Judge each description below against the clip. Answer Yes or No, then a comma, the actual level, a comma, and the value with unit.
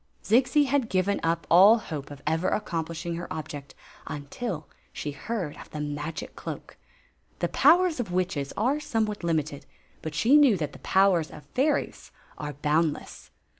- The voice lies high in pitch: No, medium, 170 Hz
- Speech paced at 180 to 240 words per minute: No, average, 155 wpm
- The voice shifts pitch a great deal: Yes, wide, 6.8 semitones